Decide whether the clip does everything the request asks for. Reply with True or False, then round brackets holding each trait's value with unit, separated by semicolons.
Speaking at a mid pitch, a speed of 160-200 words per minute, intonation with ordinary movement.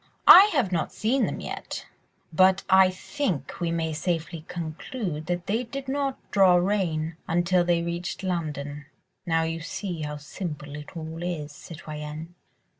False (170 Hz; 150 wpm; 3.4 semitones)